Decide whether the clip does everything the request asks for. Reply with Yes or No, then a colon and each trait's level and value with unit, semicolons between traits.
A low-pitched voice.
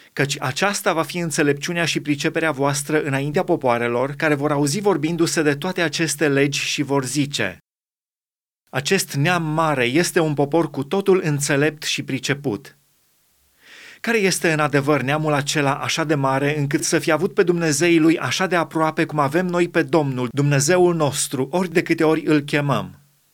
No: medium, 155 Hz